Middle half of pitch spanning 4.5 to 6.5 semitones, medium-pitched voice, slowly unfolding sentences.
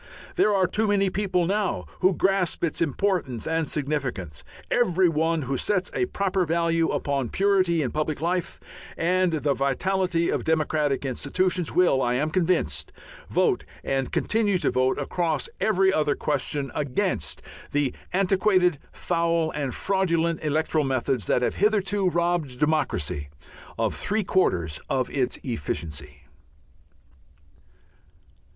Yes: average, 5.2 semitones; medium, 165 Hz; slow, 130 wpm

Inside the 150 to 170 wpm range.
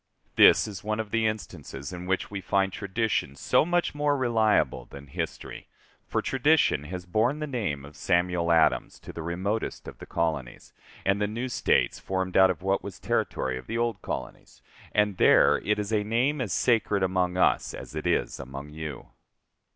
No: average, 185 wpm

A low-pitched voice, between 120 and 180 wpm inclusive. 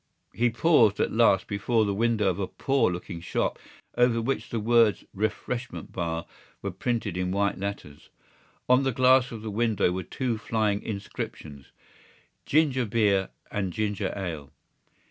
Yes: low, 105 Hz; average, 150 wpm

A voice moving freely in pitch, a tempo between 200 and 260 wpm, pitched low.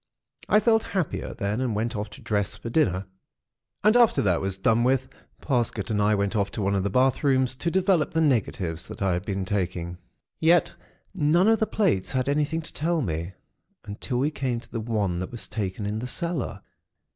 Yes: wide, 7.5 semitones; fast, 205 wpm; low, 115 Hz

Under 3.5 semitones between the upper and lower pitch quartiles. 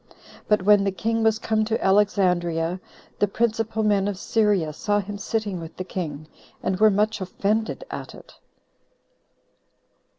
Yes: average, 2.9 semitones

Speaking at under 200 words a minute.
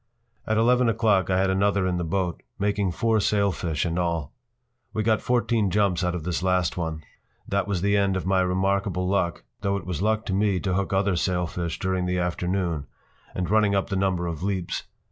No: fast, 205 wpm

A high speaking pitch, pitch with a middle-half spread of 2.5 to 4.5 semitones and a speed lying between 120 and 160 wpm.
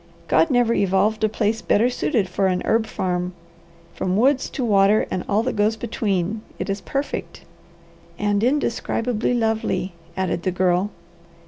Yes: high, 210 Hz; average, 3.4 semitones; average, 150 wpm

